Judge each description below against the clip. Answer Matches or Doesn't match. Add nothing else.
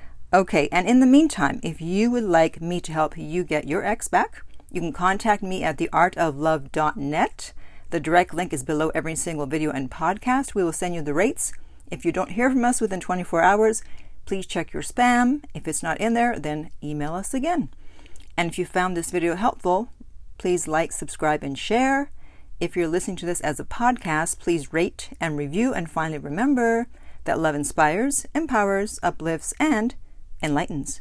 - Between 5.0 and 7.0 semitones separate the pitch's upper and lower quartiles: Matches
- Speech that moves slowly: Doesn't match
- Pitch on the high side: Doesn't match